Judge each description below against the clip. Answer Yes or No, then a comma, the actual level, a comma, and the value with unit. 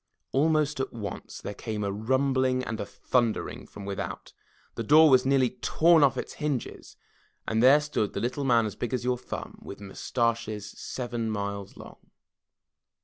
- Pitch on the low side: Yes, low, 120 Hz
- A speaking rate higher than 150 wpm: Yes, average, 165 wpm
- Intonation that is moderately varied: Yes, average, 3.9 semitones